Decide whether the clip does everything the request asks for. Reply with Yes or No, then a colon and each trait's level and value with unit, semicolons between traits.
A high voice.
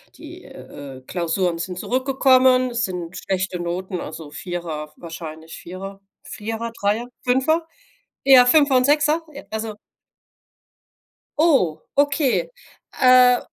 Yes: high, 215 Hz